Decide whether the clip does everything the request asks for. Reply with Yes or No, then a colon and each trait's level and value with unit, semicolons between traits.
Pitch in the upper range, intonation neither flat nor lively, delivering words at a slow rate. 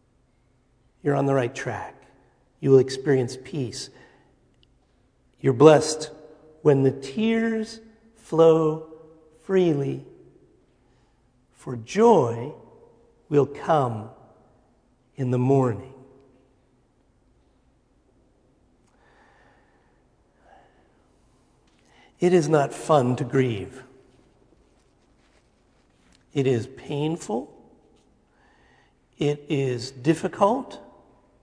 No: low, 135 Hz; average, 3.7 semitones; slow, 65 wpm